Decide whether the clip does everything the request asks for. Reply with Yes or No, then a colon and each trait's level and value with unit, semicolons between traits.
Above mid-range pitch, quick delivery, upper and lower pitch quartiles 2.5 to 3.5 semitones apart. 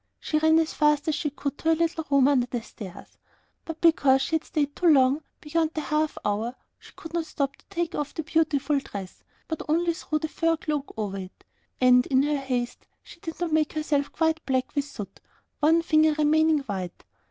Yes: very high, 300 Hz; fast, 210 wpm; average, 3.1 semitones